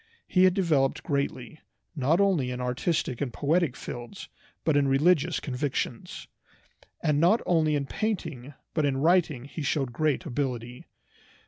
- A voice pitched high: No, medium, 145 Hz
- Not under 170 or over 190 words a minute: No, average, 140 wpm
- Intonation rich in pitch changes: No, average, 4.3 semitones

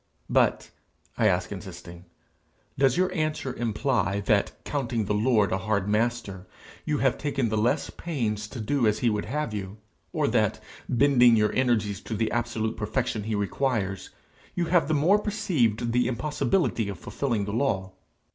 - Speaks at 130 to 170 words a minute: Yes, average, 165 wpm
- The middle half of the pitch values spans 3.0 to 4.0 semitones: No, average, 4.7 semitones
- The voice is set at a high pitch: No, low, 115 Hz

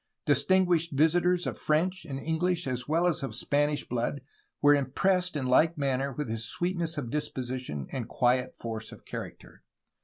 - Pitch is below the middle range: No, medium, 145 Hz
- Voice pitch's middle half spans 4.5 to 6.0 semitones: Yes, average, 4.8 semitones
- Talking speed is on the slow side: No, average, 165 wpm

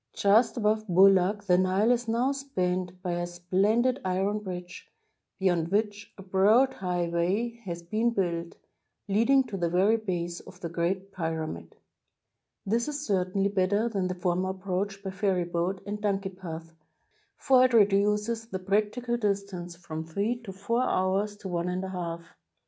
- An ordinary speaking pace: Yes, average, 160 wpm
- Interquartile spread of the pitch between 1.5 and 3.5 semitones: Yes, average, 2.9 semitones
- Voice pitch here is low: No, high, 195 Hz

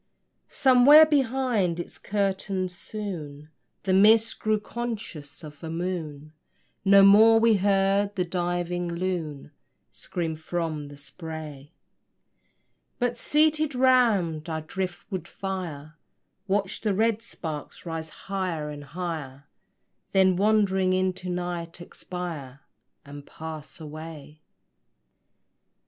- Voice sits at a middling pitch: Yes, medium, 180 Hz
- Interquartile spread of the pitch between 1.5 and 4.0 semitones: No, average, 4.4 semitones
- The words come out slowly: Yes, slow, 105 wpm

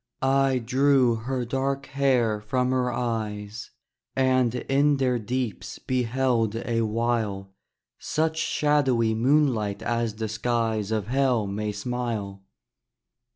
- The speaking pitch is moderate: No, low, 120 Hz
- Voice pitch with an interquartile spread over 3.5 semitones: No, average, 3.1 semitones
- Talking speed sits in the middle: No, slow, 110 wpm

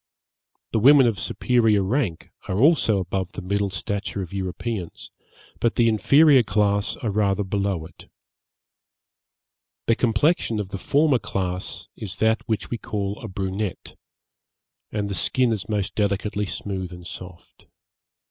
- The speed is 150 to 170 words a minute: No, average, 140 wpm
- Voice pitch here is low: Yes, low, 105 Hz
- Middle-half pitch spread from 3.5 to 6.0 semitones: No, average, 3.1 semitones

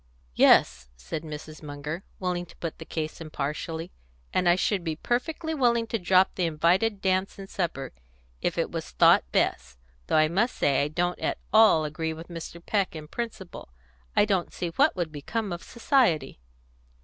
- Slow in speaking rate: No, average, 175 wpm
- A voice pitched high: No, medium, 170 Hz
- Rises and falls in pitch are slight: No, average, 4.2 semitones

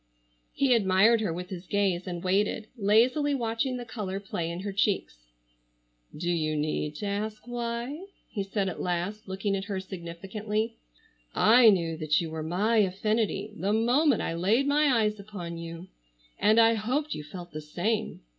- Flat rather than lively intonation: No, average, 4.3 semitones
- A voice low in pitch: No, high, 205 Hz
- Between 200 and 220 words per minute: No, average, 170 wpm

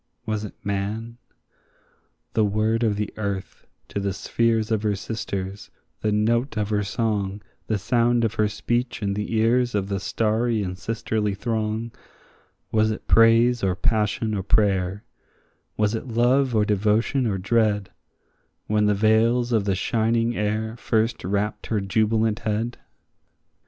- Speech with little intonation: Yes, narrow, 1.9 semitones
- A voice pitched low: Yes, low, 110 Hz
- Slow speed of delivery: No, average, 145 wpm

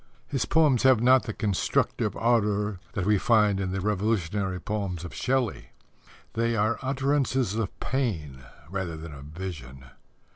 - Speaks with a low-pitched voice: Yes, low, 105 Hz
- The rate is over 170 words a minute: No, average, 145 wpm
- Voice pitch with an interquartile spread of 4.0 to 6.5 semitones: Yes, average, 4.8 semitones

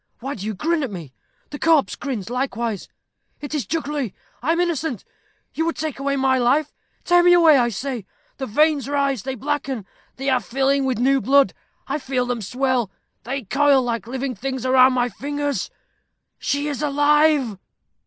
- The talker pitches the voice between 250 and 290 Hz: Yes, very high, 270 Hz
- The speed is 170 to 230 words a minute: Yes, average, 175 wpm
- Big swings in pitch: No, average, 2.9 semitones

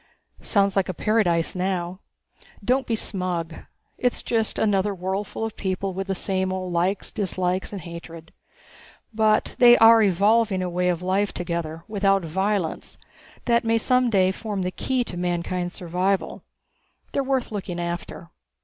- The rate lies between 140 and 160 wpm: Yes, average, 150 wpm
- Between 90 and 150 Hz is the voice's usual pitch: No, high, 190 Hz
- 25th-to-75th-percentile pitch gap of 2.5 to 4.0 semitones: Yes, average, 3.2 semitones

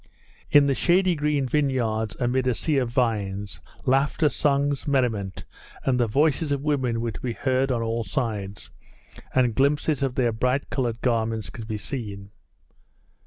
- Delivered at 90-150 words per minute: No, average, 160 wpm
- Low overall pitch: Yes, low, 125 Hz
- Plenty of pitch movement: No, average, 3.7 semitones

